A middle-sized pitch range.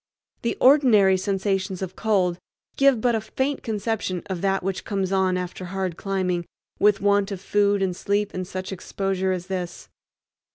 No: narrow, 1.9 semitones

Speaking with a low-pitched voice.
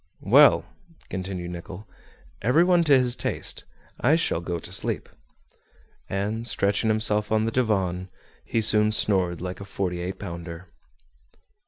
Yes: low, 100 Hz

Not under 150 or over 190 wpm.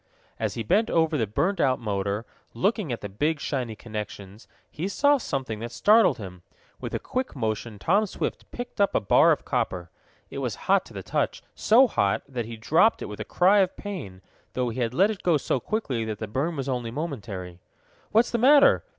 No: fast, 205 wpm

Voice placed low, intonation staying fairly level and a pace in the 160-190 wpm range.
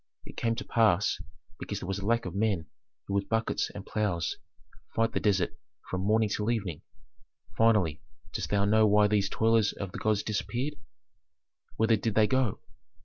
Yes: low, 105 Hz; narrow, 2.3 semitones; average, 175 wpm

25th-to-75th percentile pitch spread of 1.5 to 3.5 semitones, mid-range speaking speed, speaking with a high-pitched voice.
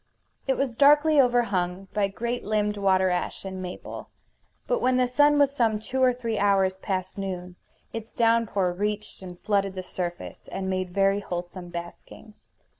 No: average, 4.3 semitones; average, 165 wpm; high, 200 Hz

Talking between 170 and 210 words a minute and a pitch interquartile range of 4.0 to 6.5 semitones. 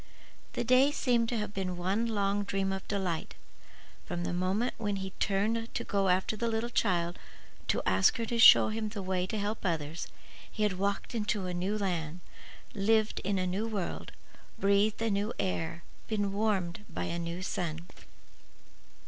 No: average, 180 wpm; average, 3.1 semitones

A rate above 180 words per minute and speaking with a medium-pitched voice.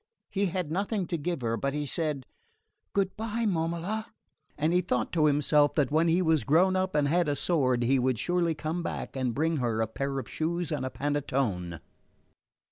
Yes: average, 200 wpm; medium, 155 Hz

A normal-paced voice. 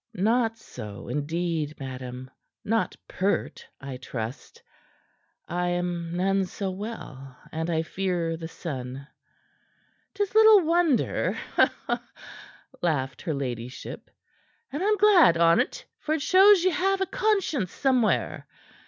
No: slow, 115 wpm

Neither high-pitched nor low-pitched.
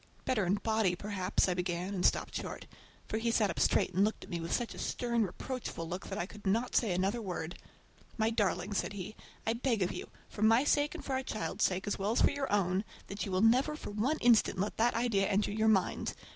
No: high, 210 Hz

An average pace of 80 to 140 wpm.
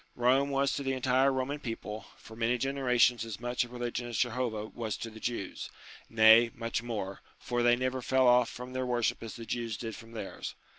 No: fast, 205 wpm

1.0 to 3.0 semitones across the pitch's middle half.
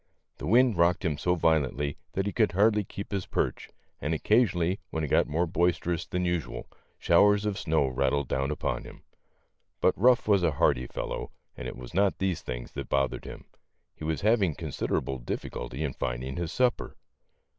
No: wide, 5.5 semitones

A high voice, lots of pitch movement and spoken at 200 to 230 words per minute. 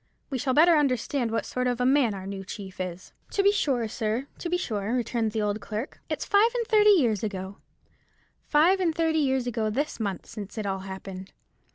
Yes: high, 240 Hz; wide, 6.5 semitones; fast, 205 wpm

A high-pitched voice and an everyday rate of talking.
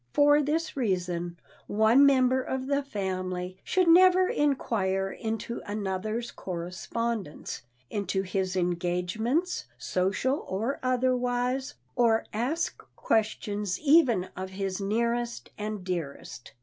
No: high, 220 Hz; slow, 105 wpm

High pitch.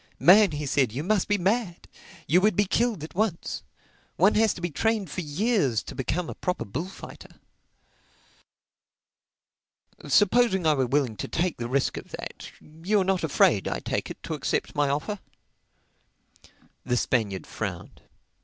No: medium, 175 Hz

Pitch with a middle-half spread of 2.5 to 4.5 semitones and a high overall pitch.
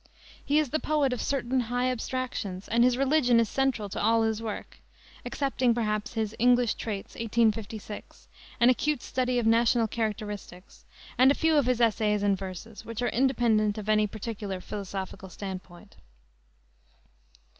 Yes: average, 3.1 semitones; high, 230 Hz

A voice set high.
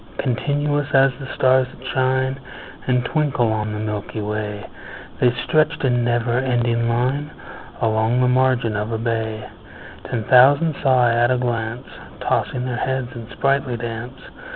No: low, 125 Hz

